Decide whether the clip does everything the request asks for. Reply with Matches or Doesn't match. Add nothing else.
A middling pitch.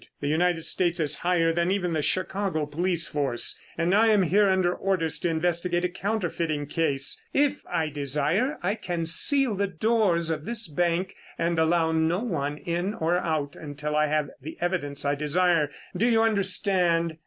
Matches